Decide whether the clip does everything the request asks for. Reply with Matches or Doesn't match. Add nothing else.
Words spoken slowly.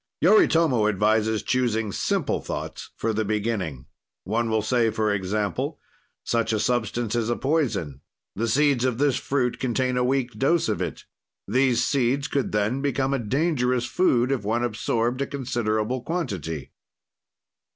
Doesn't match